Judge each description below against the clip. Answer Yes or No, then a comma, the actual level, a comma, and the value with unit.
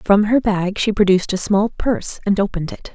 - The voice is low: No, high, 200 Hz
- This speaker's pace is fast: Yes, fast, 225 wpm